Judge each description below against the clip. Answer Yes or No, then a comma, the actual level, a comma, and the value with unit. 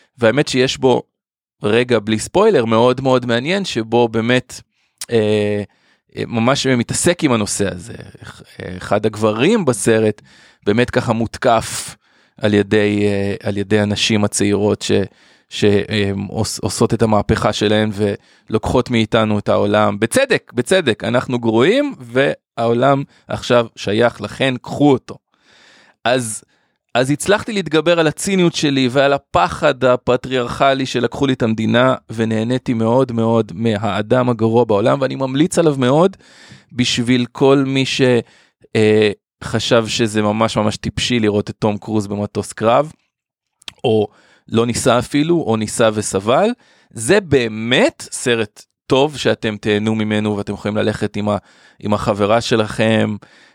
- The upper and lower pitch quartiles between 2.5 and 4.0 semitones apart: Yes, average, 3.3 semitones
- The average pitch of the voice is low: Yes, low, 115 Hz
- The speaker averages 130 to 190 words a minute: No, average, 120 wpm